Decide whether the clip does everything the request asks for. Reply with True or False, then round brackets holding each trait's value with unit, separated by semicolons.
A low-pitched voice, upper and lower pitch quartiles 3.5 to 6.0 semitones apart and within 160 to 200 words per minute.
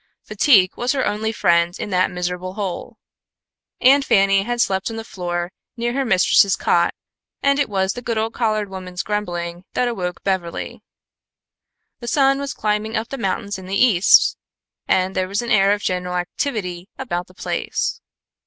False (200 Hz; 4.2 semitones; 170 wpm)